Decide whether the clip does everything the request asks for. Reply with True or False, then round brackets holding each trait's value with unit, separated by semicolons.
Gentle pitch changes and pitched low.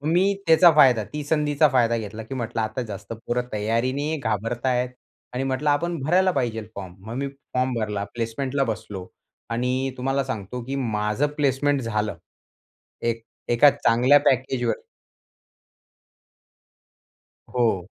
False (3.7 semitones; 125 Hz)